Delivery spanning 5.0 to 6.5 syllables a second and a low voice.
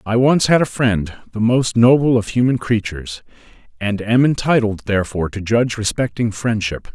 Yes: 5.2 syllables/s; low, 115 Hz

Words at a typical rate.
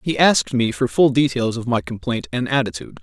No: fast, 220 wpm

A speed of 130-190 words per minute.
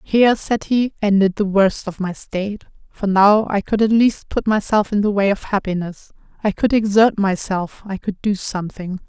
No: average, 200 wpm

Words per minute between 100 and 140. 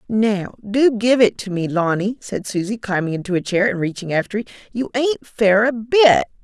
No: fast, 205 wpm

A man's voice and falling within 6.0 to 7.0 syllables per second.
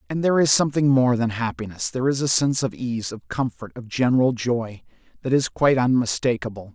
Yes: male; 6.1 syllables/s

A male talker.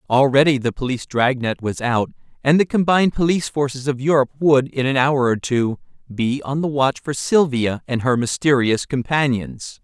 Yes: male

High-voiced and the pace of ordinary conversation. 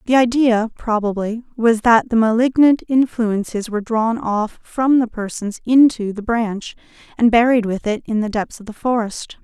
Yes: high, 230 Hz; average, 170 wpm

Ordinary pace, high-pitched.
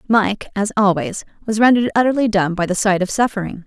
Yes: average, 195 wpm; high, 205 Hz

